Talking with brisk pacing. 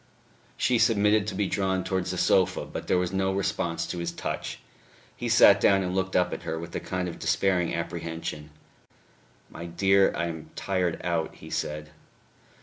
No: average, 180 wpm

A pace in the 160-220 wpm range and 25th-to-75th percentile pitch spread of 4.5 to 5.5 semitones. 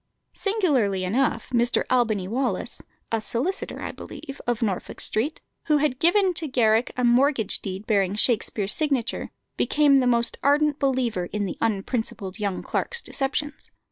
No: average, 145 wpm; average, 5.2 semitones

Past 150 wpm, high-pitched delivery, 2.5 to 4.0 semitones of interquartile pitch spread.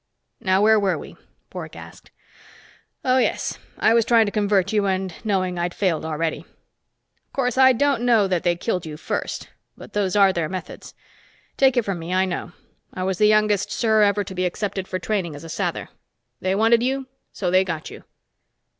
Yes: average, 195 wpm; high, 195 Hz; average, 3.2 semitones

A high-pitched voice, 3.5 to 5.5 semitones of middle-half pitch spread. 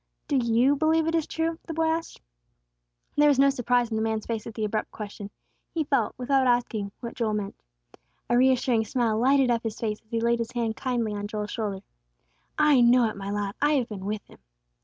Yes: high, 235 Hz; average, 4.0 semitones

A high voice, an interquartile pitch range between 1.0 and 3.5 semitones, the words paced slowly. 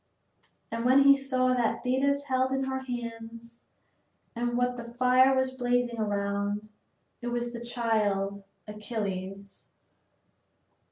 Yes: high, 240 Hz; average, 3.1 semitones; slow, 120 wpm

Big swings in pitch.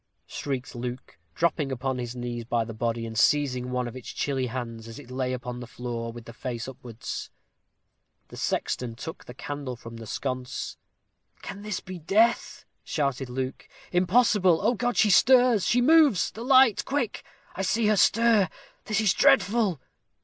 Yes: wide, 9.0 semitones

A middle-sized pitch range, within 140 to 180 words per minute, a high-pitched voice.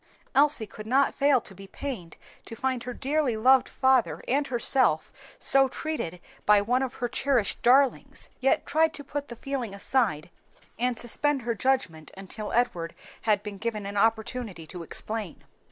Yes: average, 4.6 semitones; average, 165 wpm; high, 240 Hz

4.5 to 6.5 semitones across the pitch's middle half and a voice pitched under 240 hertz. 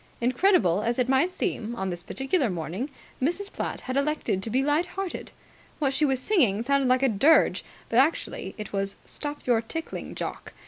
No: average, 5.3 semitones; very high, 265 Hz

